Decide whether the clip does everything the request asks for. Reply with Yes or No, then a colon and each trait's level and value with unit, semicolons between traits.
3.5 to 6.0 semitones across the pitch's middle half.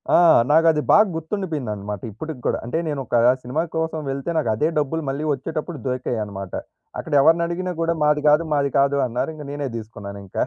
Yes: average, 4.9 semitones